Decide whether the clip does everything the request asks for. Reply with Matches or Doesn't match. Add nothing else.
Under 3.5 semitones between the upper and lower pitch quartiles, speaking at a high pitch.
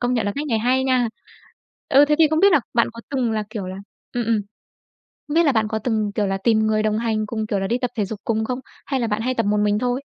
Matches